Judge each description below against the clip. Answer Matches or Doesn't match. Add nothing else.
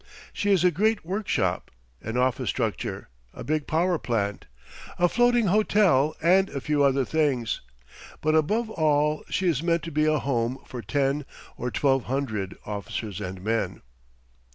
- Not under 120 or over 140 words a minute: Doesn't match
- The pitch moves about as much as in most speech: Doesn't match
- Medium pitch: Matches